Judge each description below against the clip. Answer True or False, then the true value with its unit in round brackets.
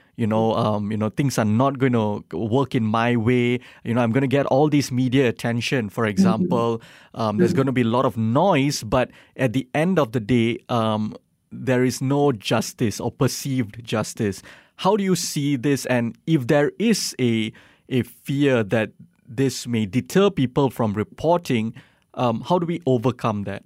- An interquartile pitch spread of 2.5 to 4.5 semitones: True (3.6 semitones)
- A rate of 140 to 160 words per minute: False (190 wpm)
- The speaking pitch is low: True (125 Hz)